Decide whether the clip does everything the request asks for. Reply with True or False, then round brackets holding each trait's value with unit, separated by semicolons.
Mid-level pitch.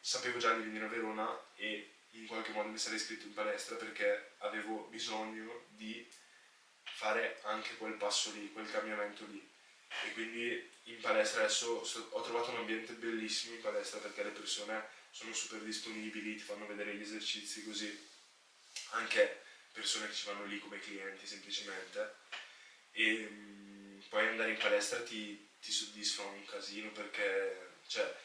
False (110 Hz)